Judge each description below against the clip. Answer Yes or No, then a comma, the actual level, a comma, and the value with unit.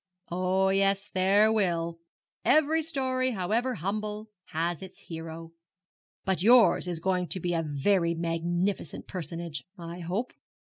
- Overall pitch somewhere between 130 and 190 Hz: Yes, medium, 185 Hz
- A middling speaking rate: No, slow, 130 wpm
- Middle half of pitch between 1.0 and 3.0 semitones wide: No, average, 3.9 semitones